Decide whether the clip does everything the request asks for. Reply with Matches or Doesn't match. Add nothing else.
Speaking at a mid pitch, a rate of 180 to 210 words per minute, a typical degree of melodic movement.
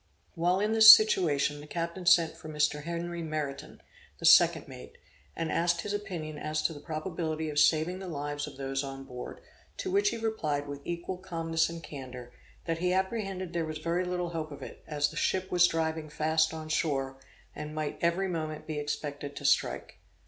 Matches